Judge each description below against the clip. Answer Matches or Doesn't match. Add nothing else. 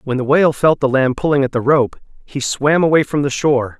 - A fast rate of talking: Matches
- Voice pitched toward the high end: Doesn't match